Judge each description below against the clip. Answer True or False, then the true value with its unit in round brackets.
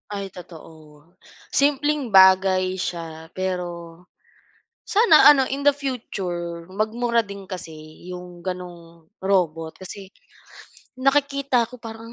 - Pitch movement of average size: False (6.0 semitones)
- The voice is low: False (190 Hz)